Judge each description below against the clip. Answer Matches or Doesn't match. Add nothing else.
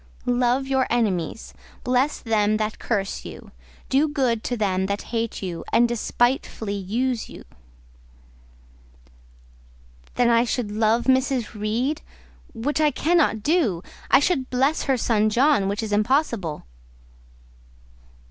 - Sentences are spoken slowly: Matches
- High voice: Matches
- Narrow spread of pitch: Doesn't match